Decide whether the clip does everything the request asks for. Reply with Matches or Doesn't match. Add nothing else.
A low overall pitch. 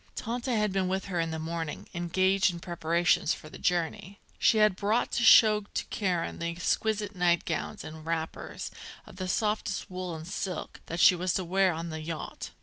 Doesn't match